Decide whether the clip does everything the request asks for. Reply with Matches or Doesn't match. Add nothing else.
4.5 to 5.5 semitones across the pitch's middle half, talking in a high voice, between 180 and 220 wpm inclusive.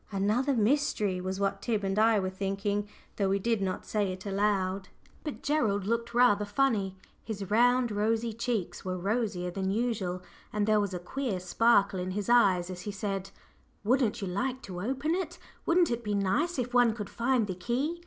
Doesn't match